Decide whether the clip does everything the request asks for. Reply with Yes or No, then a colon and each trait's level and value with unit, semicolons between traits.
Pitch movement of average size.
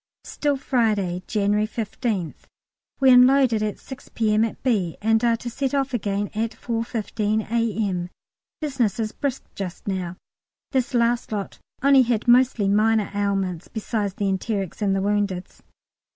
Yes: average, 3.3 semitones